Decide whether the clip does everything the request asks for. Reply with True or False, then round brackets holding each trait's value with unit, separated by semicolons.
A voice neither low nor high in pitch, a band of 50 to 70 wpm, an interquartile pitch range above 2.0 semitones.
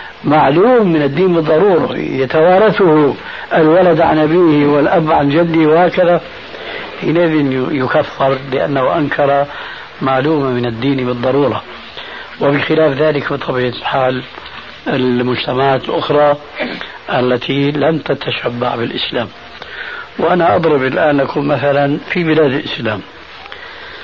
False (145 Hz; 95 wpm; 2.9 semitones)